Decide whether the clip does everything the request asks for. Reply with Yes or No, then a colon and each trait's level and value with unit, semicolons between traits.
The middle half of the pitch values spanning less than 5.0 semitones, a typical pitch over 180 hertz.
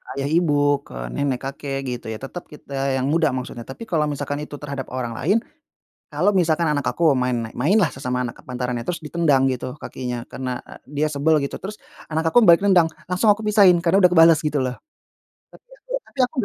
No: average, 4.4 semitones; medium, 145 Hz